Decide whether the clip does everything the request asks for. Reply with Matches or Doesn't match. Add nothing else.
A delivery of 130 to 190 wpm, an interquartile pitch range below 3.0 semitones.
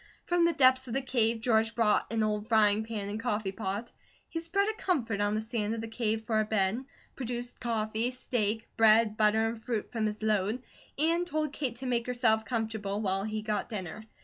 Doesn't match